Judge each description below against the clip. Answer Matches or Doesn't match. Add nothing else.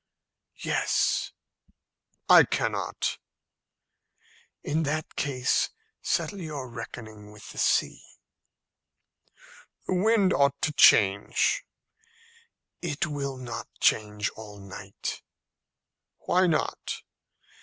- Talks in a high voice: Doesn't match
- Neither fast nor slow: Doesn't match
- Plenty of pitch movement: Matches